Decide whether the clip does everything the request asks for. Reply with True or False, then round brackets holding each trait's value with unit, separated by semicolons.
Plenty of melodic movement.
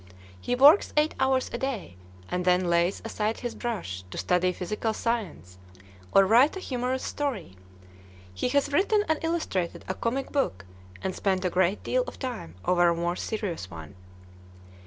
True (7.0 semitones)